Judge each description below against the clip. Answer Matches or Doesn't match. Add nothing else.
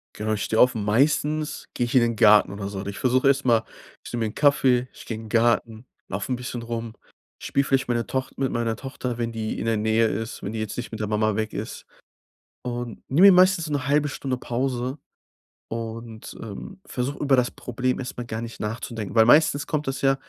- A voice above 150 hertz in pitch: Doesn't match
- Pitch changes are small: Doesn't match